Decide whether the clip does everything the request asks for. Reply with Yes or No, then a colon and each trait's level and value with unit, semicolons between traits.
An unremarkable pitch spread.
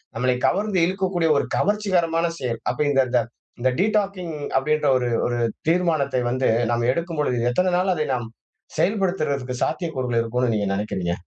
No: wide, 6.5 semitones